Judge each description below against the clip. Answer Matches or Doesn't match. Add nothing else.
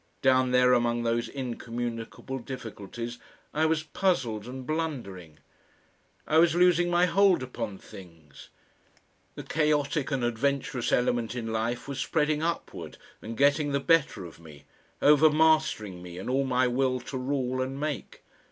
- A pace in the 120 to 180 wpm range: Matches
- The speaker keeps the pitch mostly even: Doesn't match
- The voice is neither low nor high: Doesn't match